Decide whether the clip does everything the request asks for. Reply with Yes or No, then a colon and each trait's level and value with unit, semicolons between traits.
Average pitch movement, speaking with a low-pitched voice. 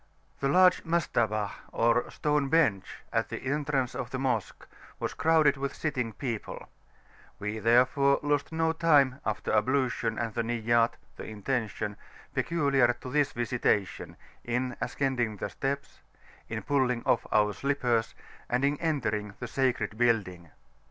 Yes: average, 3.8 semitones; low, 125 Hz